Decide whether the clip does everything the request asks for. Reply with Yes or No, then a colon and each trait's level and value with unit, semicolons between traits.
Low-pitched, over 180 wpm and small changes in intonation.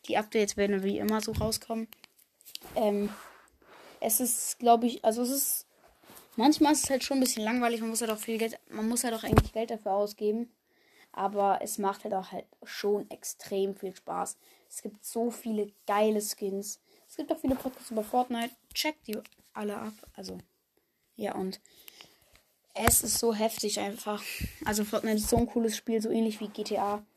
No: high, 220 Hz; fast, 190 wpm; narrow, 2.3 semitones